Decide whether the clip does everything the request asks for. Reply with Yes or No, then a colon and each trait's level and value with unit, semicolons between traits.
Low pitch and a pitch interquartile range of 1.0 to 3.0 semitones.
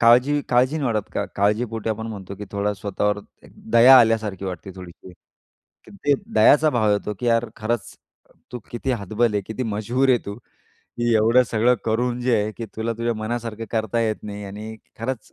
Yes: low, 110 Hz; narrow, 2.6 semitones